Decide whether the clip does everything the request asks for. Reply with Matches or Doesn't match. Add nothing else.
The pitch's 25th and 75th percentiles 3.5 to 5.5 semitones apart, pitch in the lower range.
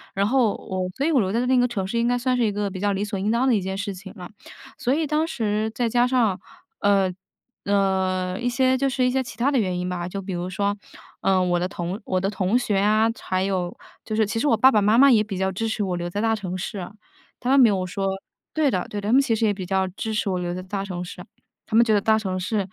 Doesn't match